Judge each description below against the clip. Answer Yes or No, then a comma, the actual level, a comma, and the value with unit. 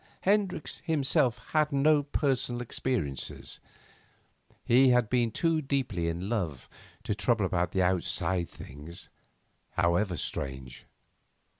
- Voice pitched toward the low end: Yes, low, 115 Hz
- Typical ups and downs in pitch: No, wide, 7.9 semitones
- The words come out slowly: Yes, slow, 105 wpm